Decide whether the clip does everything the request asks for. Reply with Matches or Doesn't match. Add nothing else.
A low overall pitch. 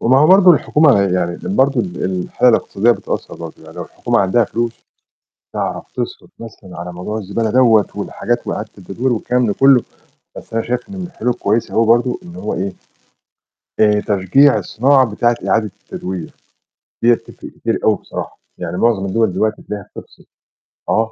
Matches